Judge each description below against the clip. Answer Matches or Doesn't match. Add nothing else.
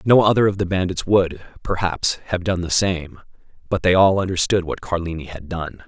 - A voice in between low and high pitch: Doesn't match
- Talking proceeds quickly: Doesn't match